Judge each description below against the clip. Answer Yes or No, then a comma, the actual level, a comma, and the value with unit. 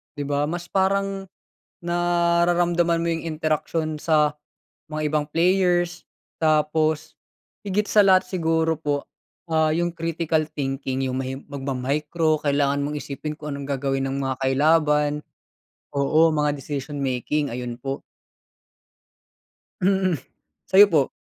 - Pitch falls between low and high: Yes, medium, 155 Hz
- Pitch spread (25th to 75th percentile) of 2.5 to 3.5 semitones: Yes, average, 3.2 semitones